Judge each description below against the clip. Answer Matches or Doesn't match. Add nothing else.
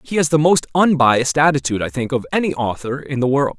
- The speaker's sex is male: Matches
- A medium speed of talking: Doesn't match